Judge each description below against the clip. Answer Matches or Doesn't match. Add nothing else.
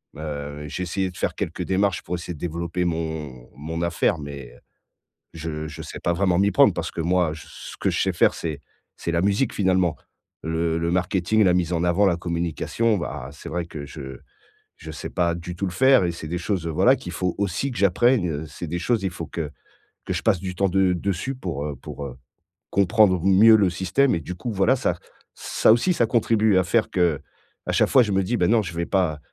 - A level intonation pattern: Doesn't match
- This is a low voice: Matches